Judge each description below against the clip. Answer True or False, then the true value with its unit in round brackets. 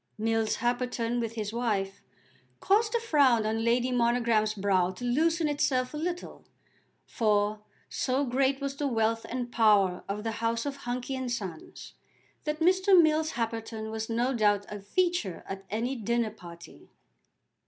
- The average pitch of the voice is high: True (235 Hz)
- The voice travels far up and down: False (3.9 semitones)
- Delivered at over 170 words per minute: False (155 wpm)